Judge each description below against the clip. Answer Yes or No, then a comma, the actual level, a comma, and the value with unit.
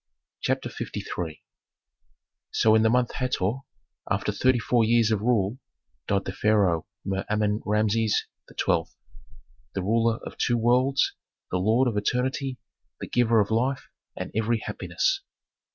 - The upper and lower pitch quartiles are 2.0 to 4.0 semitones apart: Yes, average, 3.1 semitones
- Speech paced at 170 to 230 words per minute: No, slow, 135 wpm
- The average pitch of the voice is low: Yes, low, 110 Hz